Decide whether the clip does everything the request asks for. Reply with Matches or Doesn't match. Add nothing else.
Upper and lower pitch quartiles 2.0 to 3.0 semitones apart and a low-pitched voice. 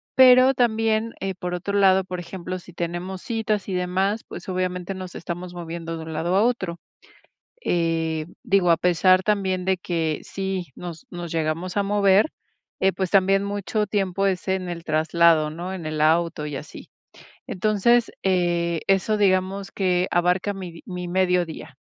Doesn't match